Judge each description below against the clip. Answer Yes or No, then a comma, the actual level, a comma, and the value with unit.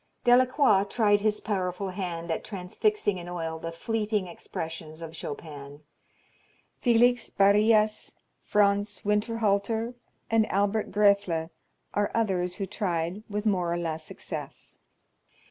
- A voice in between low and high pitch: No, high, 200 Hz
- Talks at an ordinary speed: No, slow, 115 wpm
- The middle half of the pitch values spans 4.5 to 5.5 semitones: No, average, 3.8 semitones